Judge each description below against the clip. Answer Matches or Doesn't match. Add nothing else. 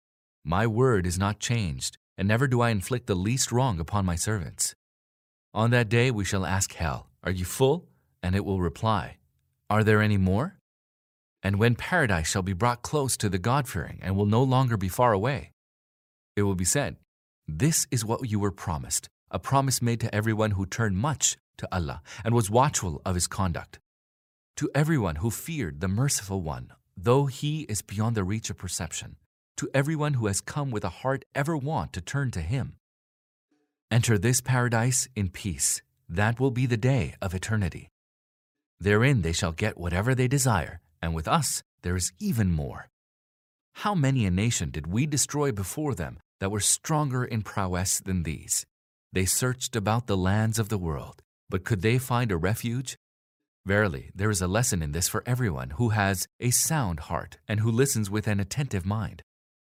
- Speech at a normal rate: Matches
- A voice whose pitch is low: Matches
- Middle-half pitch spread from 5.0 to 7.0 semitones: Matches